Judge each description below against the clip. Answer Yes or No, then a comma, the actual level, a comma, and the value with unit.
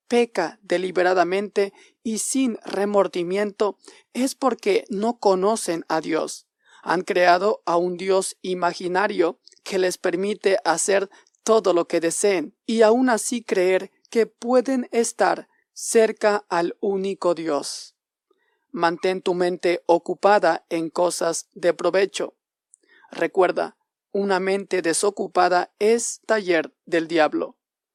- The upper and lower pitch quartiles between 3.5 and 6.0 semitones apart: Yes, average, 3.9 semitones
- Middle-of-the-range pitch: No, high, 195 Hz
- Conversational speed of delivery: No, slow, 110 wpm